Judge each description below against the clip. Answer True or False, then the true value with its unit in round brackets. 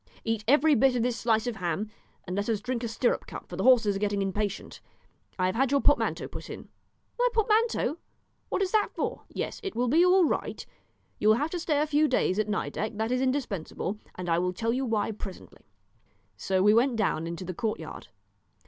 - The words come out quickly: True (215 wpm)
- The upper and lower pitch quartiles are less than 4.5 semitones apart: False (5.5 semitones)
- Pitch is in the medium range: False (230 Hz)